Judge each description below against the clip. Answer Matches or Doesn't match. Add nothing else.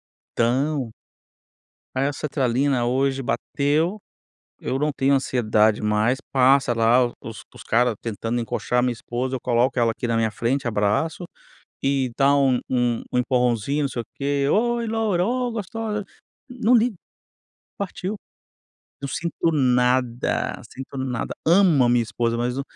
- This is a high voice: Doesn't match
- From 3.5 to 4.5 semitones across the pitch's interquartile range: Matches